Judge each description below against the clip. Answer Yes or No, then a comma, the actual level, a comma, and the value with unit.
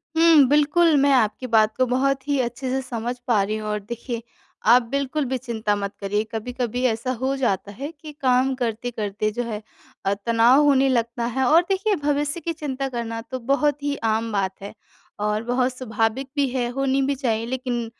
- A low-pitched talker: No, very high, 250 Hz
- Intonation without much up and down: No, average, 3.4 semitones